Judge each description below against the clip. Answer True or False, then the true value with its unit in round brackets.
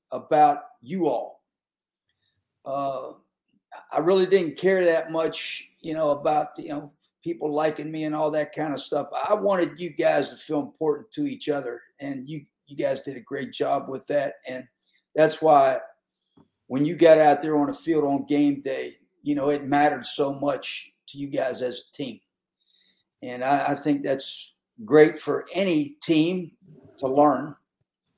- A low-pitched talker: False (150 Hz)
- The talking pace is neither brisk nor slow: True (175 wpm)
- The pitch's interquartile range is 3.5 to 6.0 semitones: False (2.8 semitones)